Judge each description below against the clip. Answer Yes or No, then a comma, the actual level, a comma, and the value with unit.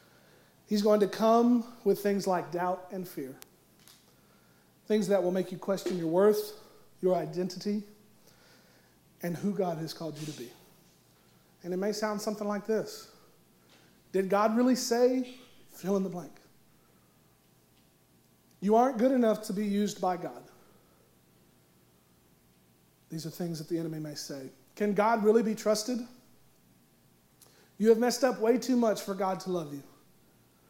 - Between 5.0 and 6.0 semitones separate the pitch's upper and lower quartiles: Yes, wide, 5.6 semitones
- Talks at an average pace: Yes, average, 150 wpm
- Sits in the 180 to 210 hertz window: Yes, high, 190 Hz